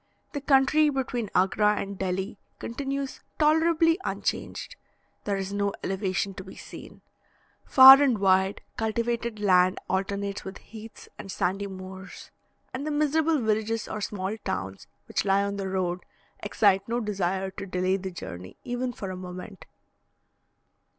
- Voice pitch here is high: Yes, high, 200 Hz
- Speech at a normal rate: Yes, average, 145 wpm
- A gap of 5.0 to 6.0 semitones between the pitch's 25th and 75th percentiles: No, average, 4.2 semitones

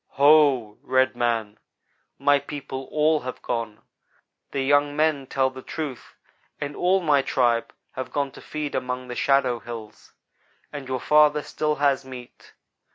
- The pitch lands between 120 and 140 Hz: Yes, low, 135 Hz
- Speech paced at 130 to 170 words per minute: Yes, average, 150 wpm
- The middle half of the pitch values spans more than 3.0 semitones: No, narrow, 2.6 semitones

